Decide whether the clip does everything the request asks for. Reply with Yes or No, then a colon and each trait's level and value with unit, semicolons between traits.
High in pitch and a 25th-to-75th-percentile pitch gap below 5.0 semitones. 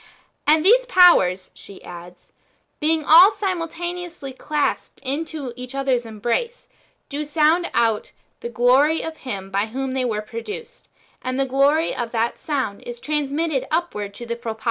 No: very high, 275 Hz; wide, 5.6 semitones